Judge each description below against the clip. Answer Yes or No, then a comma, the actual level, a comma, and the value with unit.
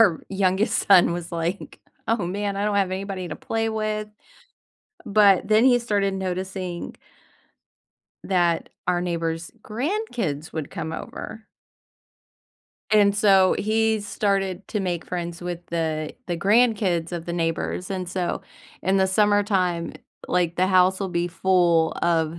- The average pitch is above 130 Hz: Yes, medium, 185 Hz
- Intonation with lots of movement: No, average, 3.0 semitones